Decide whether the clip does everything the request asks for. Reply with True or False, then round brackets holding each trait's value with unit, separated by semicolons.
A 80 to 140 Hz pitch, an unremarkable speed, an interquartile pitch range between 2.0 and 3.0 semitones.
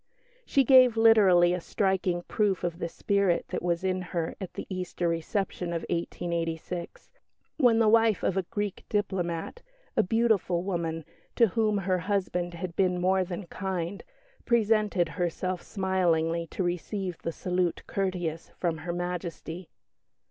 False (180 Hz; 145 wpm; 2.6 semitones)